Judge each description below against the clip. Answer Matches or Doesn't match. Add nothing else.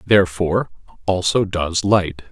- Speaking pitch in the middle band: Doesn't match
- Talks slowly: Matches